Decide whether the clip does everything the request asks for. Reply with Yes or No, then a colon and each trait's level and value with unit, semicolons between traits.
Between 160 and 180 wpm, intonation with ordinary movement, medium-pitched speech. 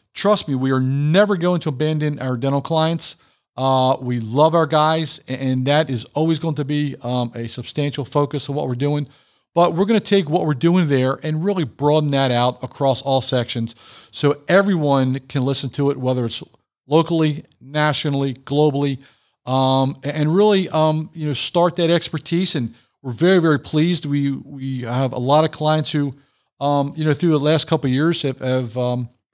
No: average, 190 wpm; average, 3.2 semitones; medium, 145 Hz